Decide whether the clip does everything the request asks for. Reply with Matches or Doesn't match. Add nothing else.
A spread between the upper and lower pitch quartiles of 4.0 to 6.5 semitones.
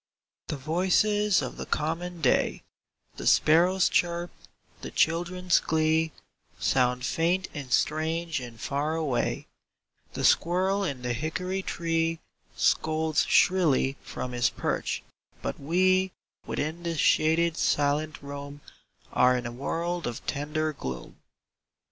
Doesn't match